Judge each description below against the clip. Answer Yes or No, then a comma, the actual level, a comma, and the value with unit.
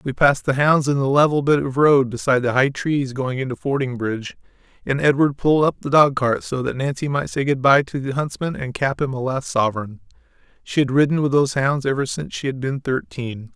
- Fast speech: Yes, fast, 230 wpm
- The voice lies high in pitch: No, low, 135 Hz